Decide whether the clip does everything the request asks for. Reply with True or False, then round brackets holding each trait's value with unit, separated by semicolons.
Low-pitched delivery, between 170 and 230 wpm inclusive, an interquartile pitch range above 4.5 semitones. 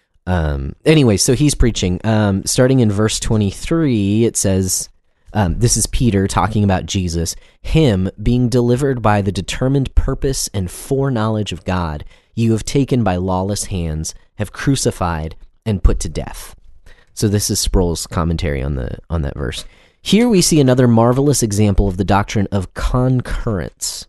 False (100 Hz; 155 wpm; 5.2 semitones)